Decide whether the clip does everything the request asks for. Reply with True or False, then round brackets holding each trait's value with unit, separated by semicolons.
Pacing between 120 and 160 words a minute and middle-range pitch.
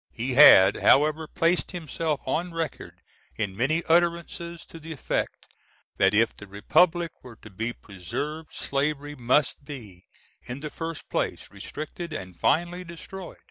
True (140 wpm; 150 Hz)